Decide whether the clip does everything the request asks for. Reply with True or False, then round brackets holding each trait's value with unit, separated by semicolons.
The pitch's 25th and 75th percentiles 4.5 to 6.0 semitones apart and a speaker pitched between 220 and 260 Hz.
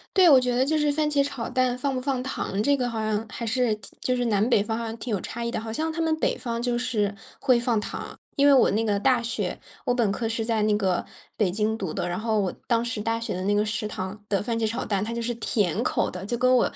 False (3.0 semitones; 230 Hz)